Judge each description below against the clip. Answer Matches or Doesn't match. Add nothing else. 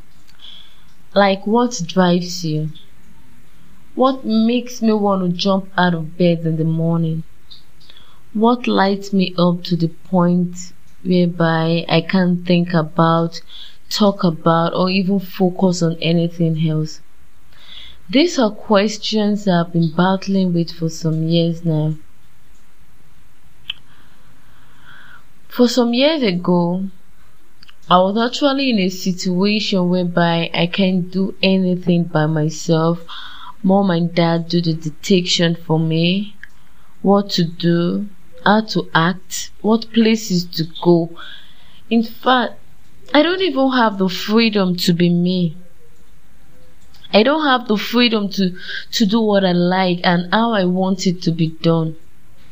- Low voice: Doesn't match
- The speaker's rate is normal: Doesn't match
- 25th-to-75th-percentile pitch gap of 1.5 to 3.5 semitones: Matches